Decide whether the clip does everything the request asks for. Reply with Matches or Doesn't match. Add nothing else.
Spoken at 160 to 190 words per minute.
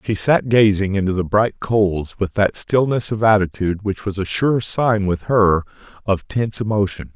Matches